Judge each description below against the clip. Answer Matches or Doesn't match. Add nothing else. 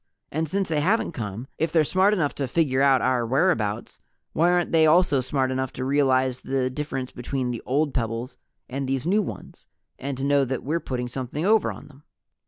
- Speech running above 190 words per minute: Matches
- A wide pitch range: Doesn't match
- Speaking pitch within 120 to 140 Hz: Matches